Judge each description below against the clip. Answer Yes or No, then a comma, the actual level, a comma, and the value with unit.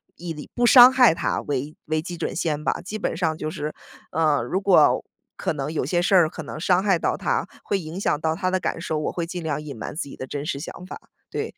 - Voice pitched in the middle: Yes, medium, 160 Hz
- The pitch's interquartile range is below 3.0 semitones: No, average, 3.3 semitones